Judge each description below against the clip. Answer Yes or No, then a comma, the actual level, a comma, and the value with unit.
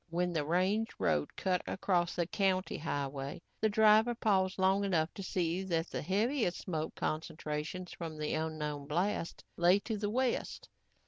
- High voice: No, medium, 180 Hz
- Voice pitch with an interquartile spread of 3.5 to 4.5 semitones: Yes, average, 3.9 semitones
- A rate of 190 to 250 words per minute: No, average, 155 wpm